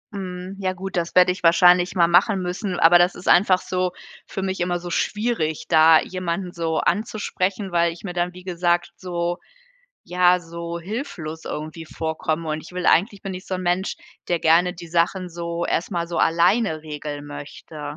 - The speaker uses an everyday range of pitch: No, narrow, 1.7 semitones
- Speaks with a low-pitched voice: No, medium, 175 Hz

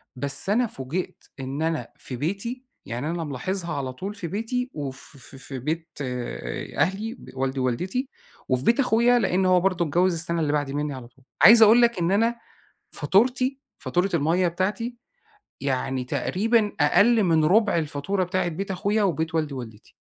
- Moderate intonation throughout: No, wide, 6.7 semitones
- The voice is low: No, medium, 170 Hz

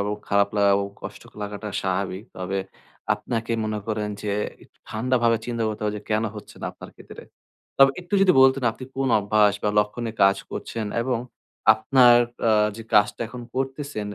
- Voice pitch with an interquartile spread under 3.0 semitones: No, average, 3.4 semitones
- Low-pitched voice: Yes, low, 110 Hz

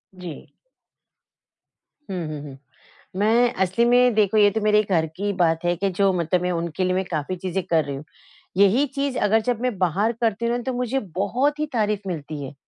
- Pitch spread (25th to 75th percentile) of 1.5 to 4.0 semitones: No, average, 5.0 semitones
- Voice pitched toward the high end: Yes, high, 195 Hz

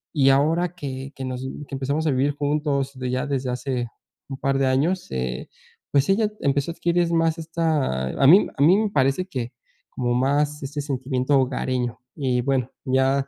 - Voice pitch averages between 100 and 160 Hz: Yes, low, 135 Hz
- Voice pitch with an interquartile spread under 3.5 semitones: Yes, average, 2.7 semitones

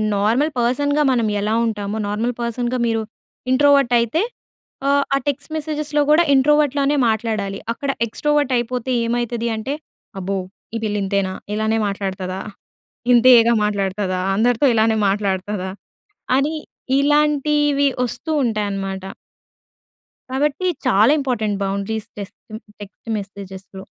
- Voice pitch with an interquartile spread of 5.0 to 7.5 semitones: Yes, wide, 5.6 semitones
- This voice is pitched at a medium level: No, high, 230 Hz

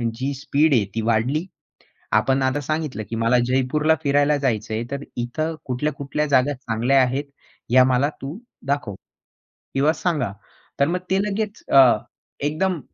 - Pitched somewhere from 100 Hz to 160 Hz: Yes, medium, 140 Hz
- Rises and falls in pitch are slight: No, average, 3.1 semitones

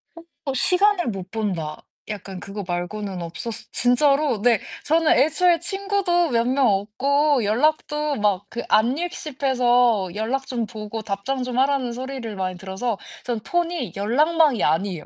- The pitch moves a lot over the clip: Yes, wide, 6.1 semitones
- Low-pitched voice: No, high, 245 Hz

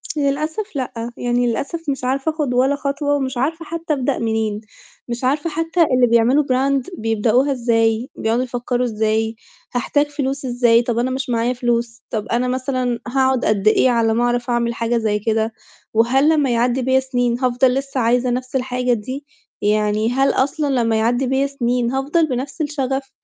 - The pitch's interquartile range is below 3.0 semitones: Yes, narrow, 2.6 semitones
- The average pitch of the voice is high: Yes, very high, 250 Hz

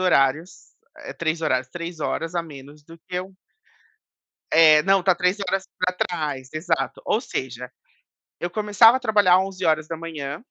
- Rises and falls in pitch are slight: No, average, 3.4 semitones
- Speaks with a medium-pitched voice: Yes, medium, 170 Hz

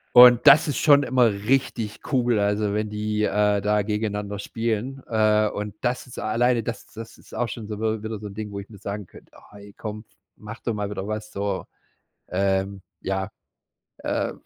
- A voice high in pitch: No, low, 105 Hz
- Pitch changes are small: Yes, narrow, 2.1 semitones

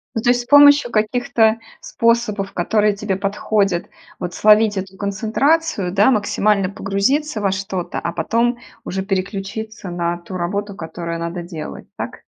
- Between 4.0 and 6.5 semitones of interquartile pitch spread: No, average, 3.2 semitones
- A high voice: Yes, high, 205 Hz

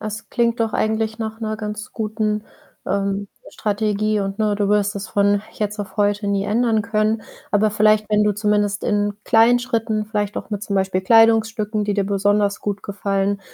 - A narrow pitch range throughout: Yes, narrow, 1.2 semitones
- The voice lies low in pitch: No, high, 210 Hz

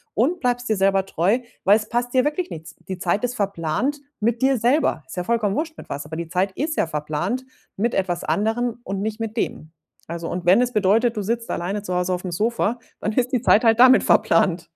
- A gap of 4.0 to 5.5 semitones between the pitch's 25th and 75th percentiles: Yes, average, 5.1 semitones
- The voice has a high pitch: Yes, high, 210 Hz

